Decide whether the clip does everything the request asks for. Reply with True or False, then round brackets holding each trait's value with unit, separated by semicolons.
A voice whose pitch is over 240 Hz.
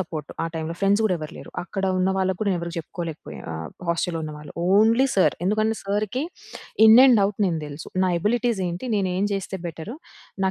False (190 Hz)